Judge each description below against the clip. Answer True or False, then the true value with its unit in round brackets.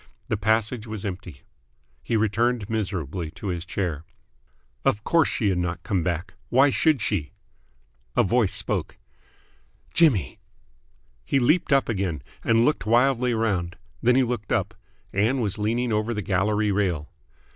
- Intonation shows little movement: False (4.4 semitones)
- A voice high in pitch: False (105 Hz)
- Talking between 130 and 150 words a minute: True (145 wpm)